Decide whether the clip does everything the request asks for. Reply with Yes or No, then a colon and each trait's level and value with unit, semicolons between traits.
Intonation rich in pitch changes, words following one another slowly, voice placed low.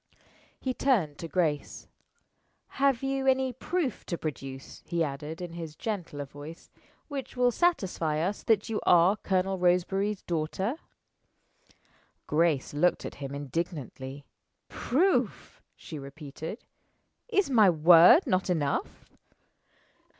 No: wide, 7.2 semitones; slow, 115 wpm; medium, 175 Hz